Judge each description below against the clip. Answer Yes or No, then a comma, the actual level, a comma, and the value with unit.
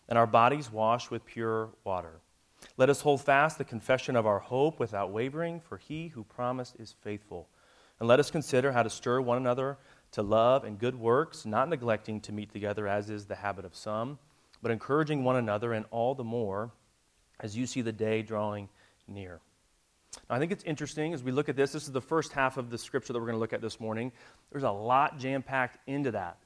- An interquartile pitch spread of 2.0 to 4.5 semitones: Yes, average, 4.0 semitones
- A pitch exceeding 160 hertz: No, low, 120 Hz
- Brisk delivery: Yes, fast, 220 wpm